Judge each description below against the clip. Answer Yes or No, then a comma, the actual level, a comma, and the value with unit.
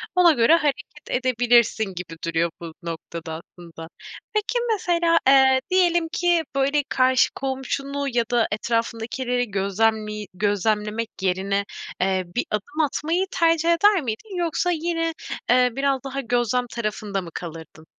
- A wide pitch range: Yes, wide, 6.7 semitones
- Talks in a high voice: Yes, high, 245 Hz